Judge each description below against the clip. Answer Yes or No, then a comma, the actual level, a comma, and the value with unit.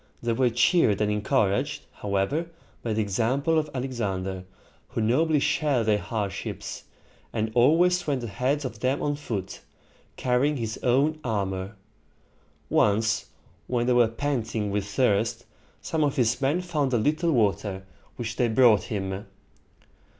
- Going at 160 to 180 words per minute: No, average, 140 wpm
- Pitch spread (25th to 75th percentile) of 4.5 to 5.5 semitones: Yes, average, 5.2 semitones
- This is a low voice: Yes, low, 120 Hz